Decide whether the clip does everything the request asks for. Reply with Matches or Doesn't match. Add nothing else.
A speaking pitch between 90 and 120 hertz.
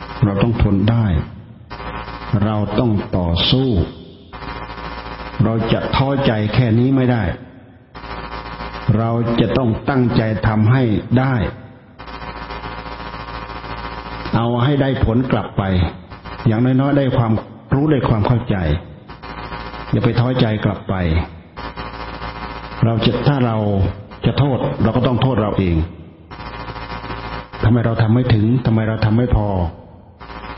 Matches